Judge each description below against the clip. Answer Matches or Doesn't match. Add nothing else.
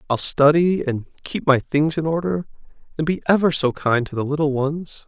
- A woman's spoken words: Doesn't match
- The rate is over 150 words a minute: Matches